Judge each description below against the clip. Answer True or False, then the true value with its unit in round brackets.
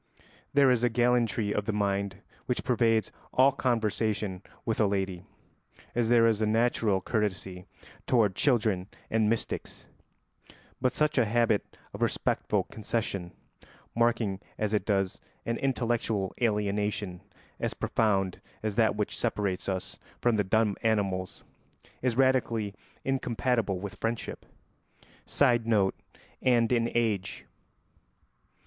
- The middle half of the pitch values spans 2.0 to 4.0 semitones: True (2.9 semitones)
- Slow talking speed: True (120 wpm)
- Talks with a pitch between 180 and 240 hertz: False (110 Hz)